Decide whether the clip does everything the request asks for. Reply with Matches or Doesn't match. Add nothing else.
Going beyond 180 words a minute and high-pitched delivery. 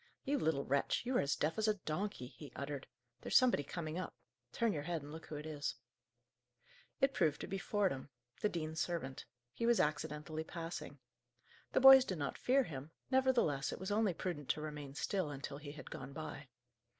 Doesn't match